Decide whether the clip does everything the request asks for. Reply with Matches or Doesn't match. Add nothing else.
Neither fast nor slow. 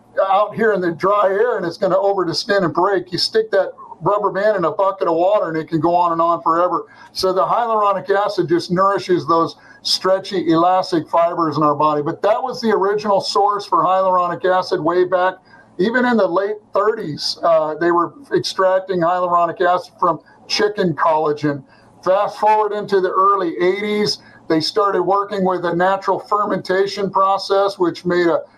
Matches